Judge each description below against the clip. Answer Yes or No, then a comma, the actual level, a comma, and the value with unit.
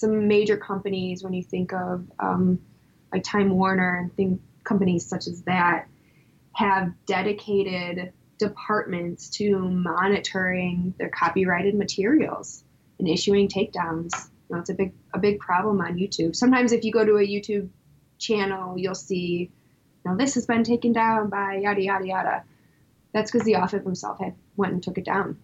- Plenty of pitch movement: No, narrow, 2.4 semitones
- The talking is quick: No, average, 155 wpm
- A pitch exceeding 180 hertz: Yes, high, 190 Hz